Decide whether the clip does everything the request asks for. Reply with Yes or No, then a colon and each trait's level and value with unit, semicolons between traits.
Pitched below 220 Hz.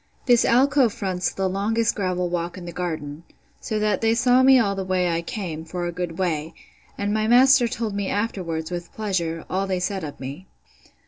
Yes: high, 190 Hz